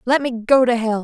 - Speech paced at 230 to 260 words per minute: No, fast, 290 wpm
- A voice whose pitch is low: No, high, 240 Hz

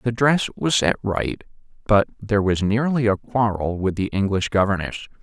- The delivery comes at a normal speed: Yes, average, 170 wpm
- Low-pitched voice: Yes, low, 105 Hz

